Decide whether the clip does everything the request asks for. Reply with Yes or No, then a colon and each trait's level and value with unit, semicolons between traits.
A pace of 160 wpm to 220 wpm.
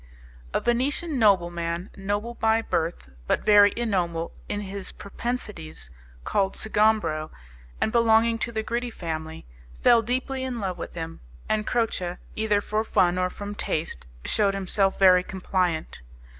No: average, 140 wpm